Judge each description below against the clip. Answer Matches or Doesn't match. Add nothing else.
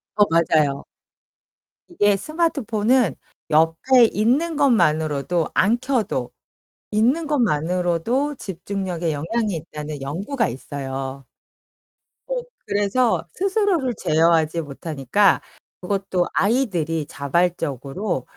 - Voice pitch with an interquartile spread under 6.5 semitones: Doesn't match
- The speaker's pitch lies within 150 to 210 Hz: Matches